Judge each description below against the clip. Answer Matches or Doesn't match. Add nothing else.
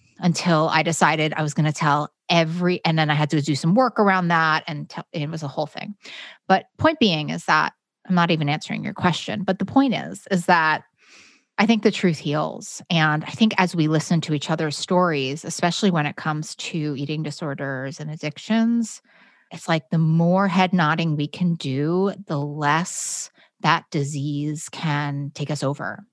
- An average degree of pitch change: Matches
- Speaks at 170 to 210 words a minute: Matches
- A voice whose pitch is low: Doesn't match